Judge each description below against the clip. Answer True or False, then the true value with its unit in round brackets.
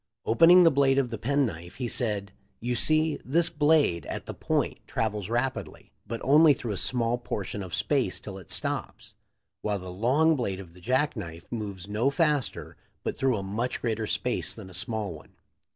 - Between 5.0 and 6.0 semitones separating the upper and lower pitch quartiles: True (5.5 semitones)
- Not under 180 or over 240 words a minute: True (190 wpm)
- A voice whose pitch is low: True (115 Hz)